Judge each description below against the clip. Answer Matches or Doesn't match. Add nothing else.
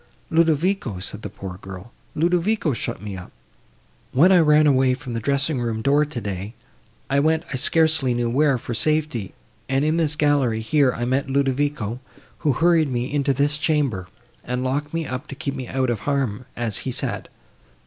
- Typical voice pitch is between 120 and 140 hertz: Matches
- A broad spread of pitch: Doesn't match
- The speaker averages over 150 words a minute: Matches